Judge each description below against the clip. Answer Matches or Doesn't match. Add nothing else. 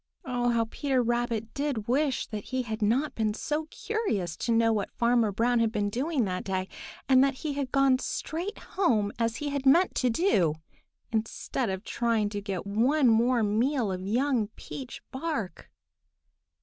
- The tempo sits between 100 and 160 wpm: Doesn't match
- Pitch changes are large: Doesn't match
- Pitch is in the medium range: Doesn't match